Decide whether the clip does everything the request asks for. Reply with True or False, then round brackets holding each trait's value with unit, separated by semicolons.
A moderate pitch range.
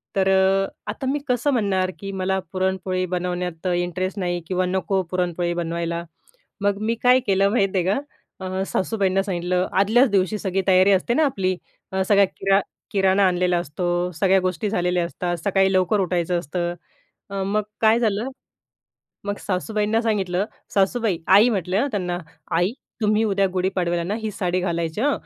False (2.0 semitones)